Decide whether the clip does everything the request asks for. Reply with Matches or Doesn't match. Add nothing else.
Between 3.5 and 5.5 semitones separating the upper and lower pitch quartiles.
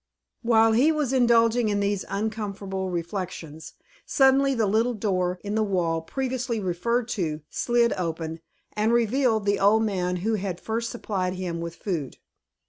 Matches